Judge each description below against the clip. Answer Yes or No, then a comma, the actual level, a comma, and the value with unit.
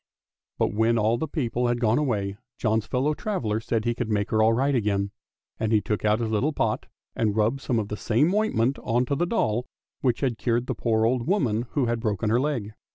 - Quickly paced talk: Yes, fast, 225 wpm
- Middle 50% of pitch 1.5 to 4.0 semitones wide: Yes, average, 3.0 semitones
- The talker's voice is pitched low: Yes, low, 115 Hz